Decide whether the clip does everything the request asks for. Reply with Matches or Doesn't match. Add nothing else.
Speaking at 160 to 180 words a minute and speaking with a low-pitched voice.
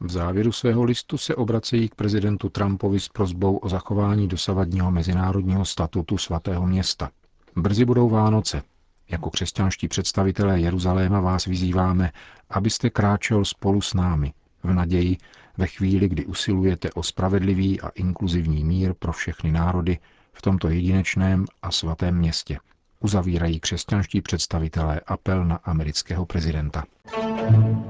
Doesn't match